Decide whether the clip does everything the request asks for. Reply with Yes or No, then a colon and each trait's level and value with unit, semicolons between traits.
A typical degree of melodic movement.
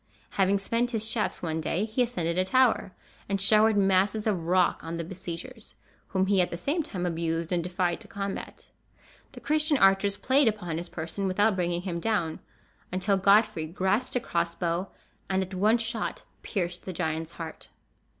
Yes: average, 3.8 semitones